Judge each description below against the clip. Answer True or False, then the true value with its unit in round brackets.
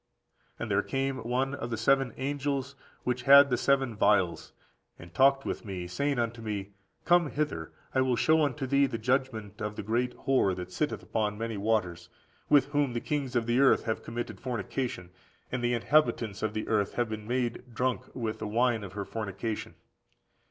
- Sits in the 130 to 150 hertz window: False (120 Hz)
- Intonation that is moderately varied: True (4.0 semitones)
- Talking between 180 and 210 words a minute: True (190 wpm)